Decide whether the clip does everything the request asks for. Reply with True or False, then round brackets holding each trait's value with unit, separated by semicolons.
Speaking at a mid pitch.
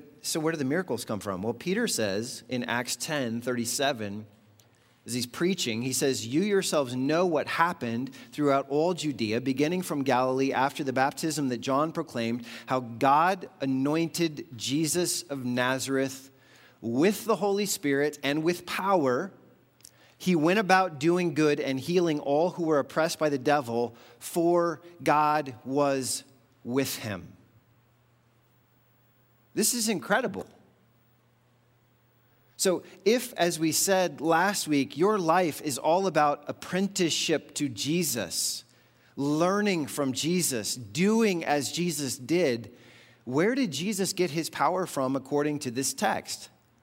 True (145 Hz)